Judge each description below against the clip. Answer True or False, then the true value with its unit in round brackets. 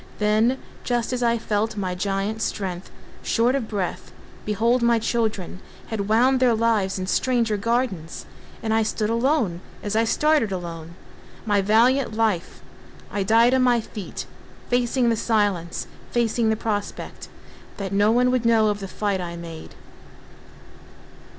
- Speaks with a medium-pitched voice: False (220 Hz)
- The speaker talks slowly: False (145 wpm)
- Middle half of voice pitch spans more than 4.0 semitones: False (3.1 semitones)